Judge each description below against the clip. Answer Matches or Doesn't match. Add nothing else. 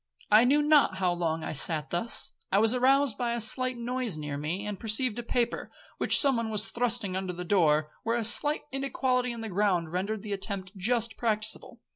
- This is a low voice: Doesn't match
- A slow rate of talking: Doesn't match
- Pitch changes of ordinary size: Matches